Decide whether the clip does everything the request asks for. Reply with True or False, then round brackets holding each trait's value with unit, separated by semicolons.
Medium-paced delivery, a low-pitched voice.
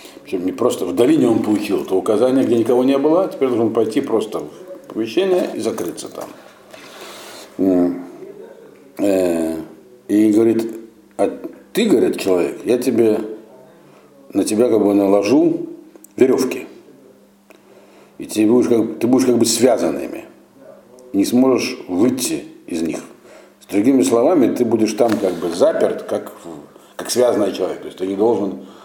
True (140 wpm; 125 Hz)